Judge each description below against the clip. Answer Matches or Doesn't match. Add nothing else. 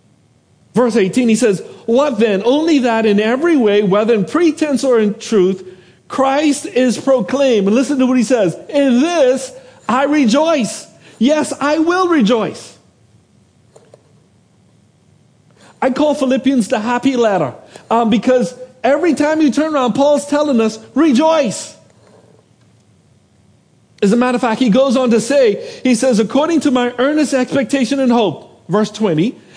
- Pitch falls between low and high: Doesn't match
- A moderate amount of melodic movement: Matches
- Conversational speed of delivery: Matches